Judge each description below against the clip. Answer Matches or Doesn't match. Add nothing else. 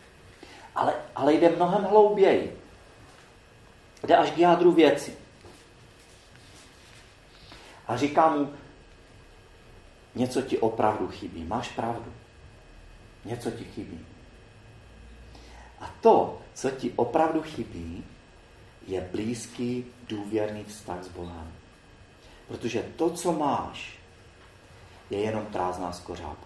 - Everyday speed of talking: Doesn't match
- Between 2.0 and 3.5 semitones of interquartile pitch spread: Doesn't match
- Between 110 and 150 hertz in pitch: Matches